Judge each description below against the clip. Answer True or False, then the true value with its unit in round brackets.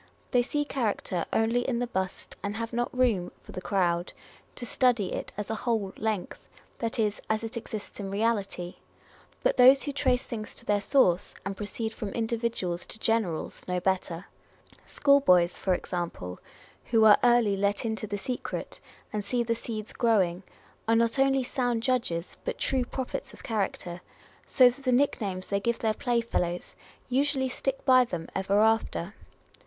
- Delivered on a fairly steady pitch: False (4.1 semitones)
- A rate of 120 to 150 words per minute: False (170 wpm)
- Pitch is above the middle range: True (225 Hz)